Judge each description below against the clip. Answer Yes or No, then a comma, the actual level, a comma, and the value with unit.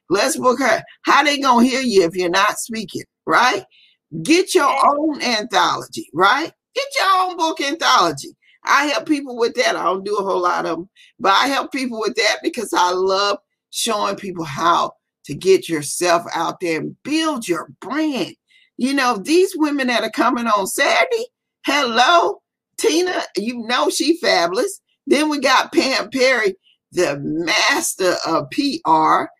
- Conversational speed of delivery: Yes, average, 165 wpm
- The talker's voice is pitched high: Yes, very high, 265 Hz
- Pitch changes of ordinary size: No, wide, 8.5 semitones